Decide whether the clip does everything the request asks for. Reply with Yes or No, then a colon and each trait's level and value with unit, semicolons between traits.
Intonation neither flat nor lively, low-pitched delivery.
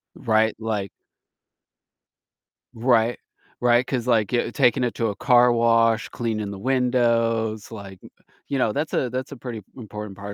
No: narrow, 2.2 semitones; low, 115 Hz